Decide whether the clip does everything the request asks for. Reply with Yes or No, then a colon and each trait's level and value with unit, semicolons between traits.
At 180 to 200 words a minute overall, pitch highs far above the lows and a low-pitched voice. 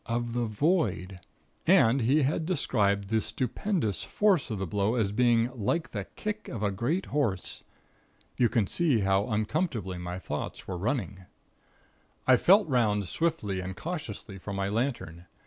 No: average, 155 wpm; wide, 6.0 semitones; low, 115 Hz